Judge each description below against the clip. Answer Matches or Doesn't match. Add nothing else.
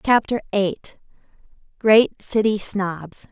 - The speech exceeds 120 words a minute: Doesn't match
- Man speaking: Doesn't match